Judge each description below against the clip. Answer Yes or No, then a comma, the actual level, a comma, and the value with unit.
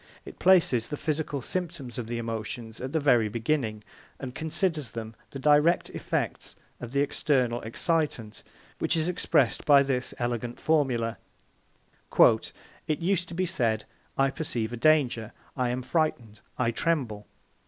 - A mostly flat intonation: No, average, 5.0 semitones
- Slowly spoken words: No, average, 145 wpm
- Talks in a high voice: No, low, 130 Hz